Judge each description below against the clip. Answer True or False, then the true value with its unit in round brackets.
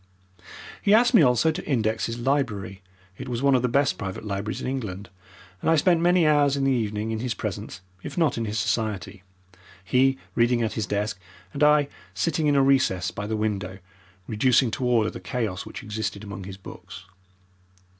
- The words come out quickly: False (195 wpm)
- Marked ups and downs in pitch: False (4.8 semitones)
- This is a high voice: False (115 Hz)